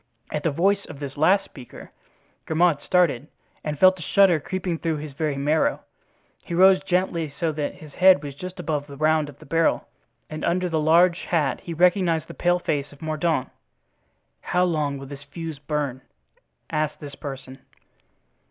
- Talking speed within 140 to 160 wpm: No, average, 175 wpm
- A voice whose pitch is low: No, medium, 155 Hz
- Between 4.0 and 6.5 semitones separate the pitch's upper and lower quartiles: No, average, 3.5 semitones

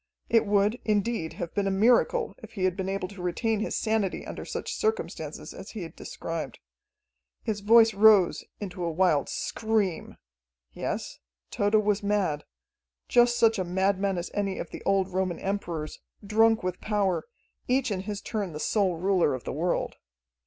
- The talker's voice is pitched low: No, high, 200 Hz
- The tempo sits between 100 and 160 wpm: No, average, 170 wpm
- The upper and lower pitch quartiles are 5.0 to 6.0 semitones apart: No, average, 3.0 semitones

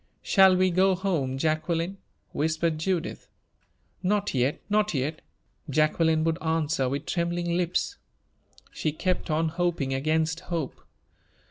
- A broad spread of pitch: No, average, 2.7 semitones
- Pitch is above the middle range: No, medium, 165 Hz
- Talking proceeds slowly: Yes, slow, 120 wpm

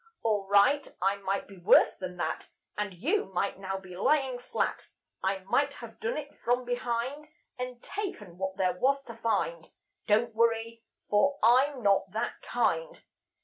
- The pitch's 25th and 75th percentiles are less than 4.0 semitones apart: No, average, 4.7 semitones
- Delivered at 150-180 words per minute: Yes, average, 160 wpm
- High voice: Yes, high, 225 Hz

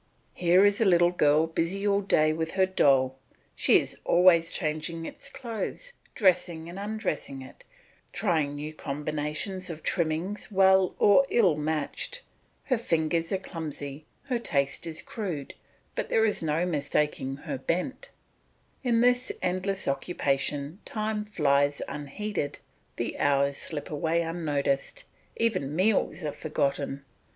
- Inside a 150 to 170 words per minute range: No, slow, 135 wpm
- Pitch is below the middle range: No, medium, 165 Hz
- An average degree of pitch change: Yes, average, 4.9 semitones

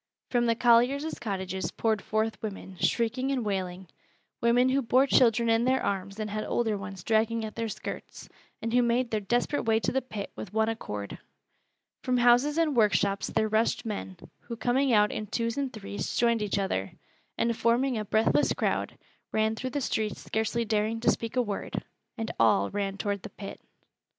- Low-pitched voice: No, high, 225 Hz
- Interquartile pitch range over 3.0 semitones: No, average, 2.7 semitones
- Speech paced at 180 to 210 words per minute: Yes, average, 185 wpm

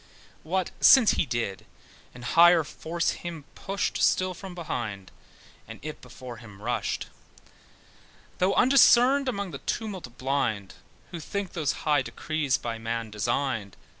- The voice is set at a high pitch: No, medium, 150 Hz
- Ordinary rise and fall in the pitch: No, wide, 7.7 semitones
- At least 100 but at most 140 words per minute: Yes, slow, 135 wpm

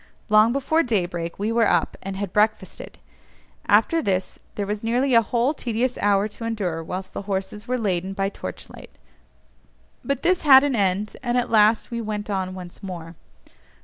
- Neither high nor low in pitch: No, high, 210 Hz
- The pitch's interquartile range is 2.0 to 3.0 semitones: No, average, 3.8 semitones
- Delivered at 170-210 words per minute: Yes, average, 180 wpm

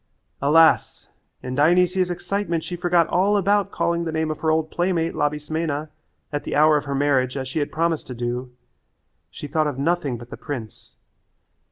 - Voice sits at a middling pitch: Yes, medium, 155 Hz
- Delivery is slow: No, average, 180 wpm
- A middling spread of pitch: Yes, average, 3.3 semitones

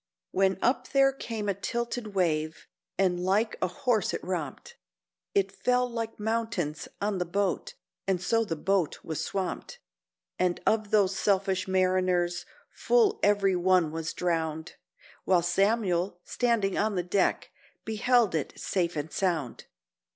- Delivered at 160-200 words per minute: No, average, 140 wpm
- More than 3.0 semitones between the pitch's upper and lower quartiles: Yes, average, 3.6 semitones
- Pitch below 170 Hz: No, high, 190 Hz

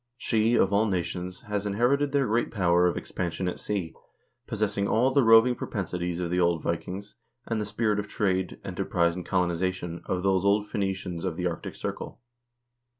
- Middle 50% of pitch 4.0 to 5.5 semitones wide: No, average, 3.2 semitones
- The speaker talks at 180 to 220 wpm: Yes, average, 185 wpm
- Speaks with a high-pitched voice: No, very low, 95 Hz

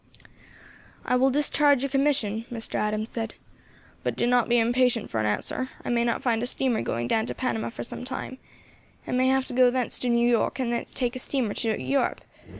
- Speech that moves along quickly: Yes, fast, 215 wpm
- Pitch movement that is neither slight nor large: No, narrow, 2.3 semitones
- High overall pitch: Yes, high, 245 Hz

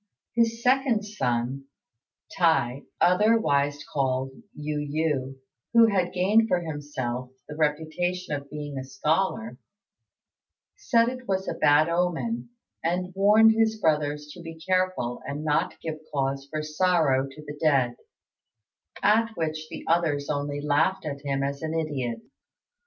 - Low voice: No, medium, 155 Hz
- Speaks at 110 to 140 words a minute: Yes, slow, 135 wpm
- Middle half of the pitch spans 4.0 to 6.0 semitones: Yes, average, 4.6 semitones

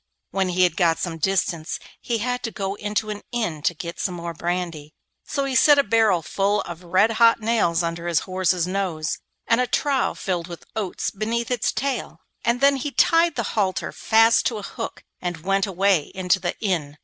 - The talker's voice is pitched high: Yes, high, 195 Hz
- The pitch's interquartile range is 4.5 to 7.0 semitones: Yes, average, 4.8 semitones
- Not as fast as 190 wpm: No, average, 200 wpm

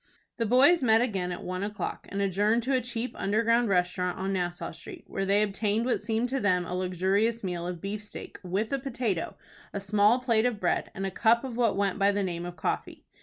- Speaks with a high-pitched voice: Yes, high, 205 Hz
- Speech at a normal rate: No, fast, 220 wpm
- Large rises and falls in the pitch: No, average, 3.7 semitones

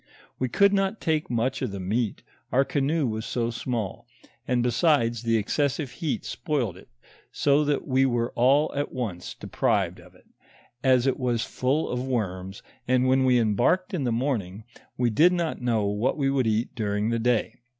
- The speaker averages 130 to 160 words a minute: No, average, 180 wpm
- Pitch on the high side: No, low, 125 Hz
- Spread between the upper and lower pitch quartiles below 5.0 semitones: Yes, average, 3.7 semitones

